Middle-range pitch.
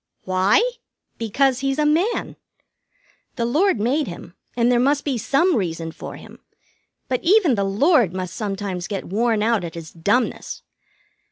No: high, 235 Hz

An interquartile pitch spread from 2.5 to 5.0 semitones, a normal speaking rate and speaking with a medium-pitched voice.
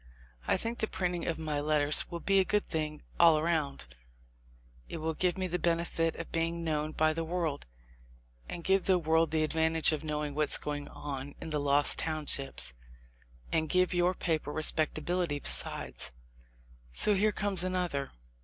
Yes: average, 2.8 semitones; average, 170 wpm; medium, 160 Hz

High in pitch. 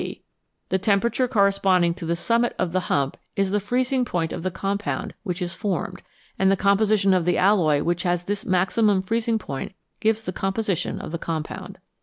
Yes: high, 195 Hz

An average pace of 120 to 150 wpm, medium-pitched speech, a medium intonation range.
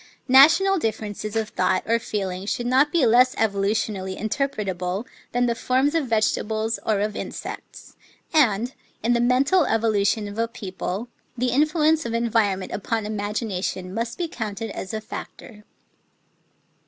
No: average, 145 wpm; high, 225 Hz; average, 3.3 semitones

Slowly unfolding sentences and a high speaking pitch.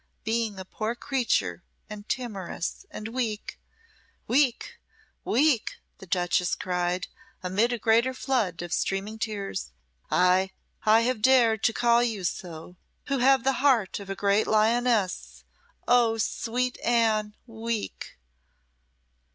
Yes: slow, 125 wpm; high, 220 Hz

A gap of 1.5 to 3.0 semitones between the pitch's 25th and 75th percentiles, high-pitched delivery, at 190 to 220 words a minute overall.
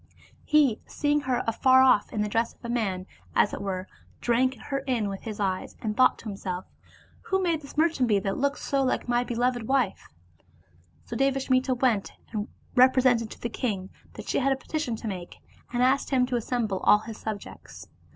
No: average, 3.8 semitones; high, 245 Hz; average, 200 wpm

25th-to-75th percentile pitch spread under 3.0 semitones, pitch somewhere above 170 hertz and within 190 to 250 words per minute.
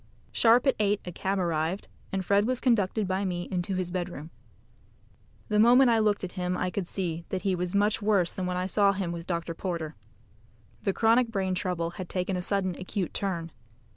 Yes: narrow, 2.4 semitones; medium, 185 Hz; average, 200 wpm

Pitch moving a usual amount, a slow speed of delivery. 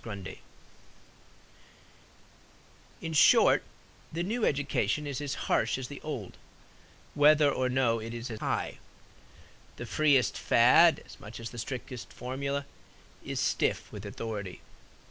Yes: average, 4.1 semitones; slow, 125 wpm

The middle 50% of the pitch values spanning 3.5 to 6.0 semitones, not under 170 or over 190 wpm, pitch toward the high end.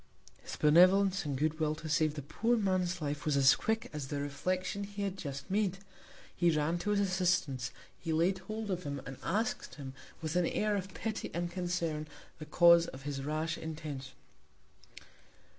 No: average, 4.1 semitones; average, 180 wpm; medium, 170 Hz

